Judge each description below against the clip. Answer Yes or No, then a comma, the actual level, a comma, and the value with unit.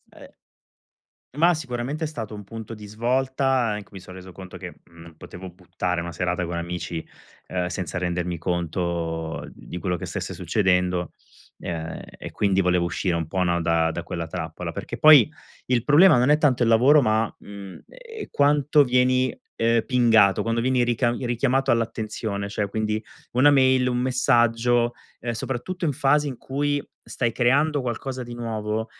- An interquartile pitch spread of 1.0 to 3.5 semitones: No, wide, 6.2 semitones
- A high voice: No, low, 115 Hz